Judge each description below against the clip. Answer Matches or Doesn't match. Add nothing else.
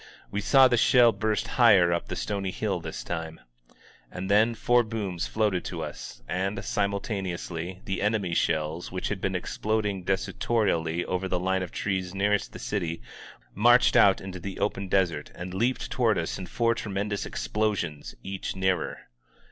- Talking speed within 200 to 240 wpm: Doesn't match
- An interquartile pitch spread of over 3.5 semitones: Doesn't match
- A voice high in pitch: Doesn't match